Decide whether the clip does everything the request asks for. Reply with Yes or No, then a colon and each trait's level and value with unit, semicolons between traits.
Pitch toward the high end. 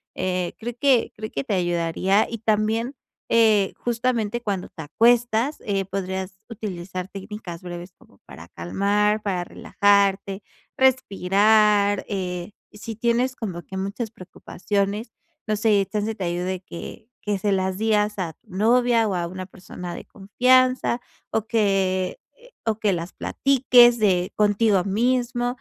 Yes: high, 205 Hz